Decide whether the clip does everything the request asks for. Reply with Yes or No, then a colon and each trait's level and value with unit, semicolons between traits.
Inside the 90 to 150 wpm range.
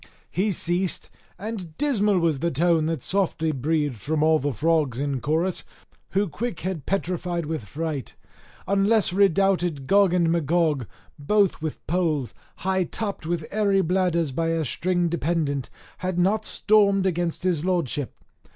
Yes: average, 145 wpm